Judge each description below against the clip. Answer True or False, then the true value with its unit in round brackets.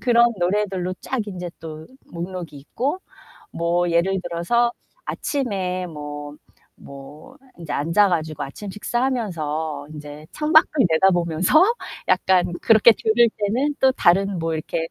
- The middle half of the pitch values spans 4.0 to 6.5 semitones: True (5.5 semitones)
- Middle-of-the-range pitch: True (180 Hz)